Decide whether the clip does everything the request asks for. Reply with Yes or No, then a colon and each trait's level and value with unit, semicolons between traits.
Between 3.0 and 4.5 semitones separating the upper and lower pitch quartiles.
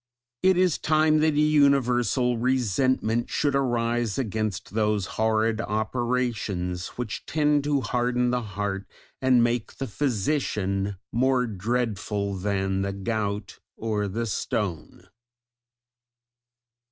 Yes: average, 3.9 semitones